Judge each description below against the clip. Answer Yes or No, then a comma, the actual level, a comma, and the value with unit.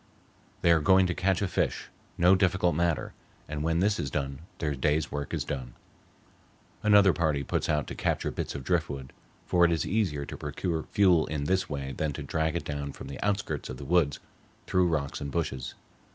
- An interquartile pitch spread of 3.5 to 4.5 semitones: Yes, average, 3.9 semitones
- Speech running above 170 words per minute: Yes, average, 200 wpm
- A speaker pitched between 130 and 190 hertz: No, very low, 80 Hz